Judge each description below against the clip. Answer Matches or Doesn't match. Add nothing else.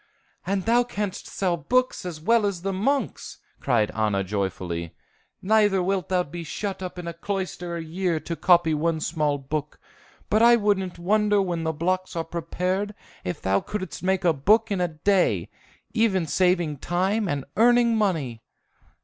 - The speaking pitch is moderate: Matches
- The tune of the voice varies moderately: Matches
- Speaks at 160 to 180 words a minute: Matches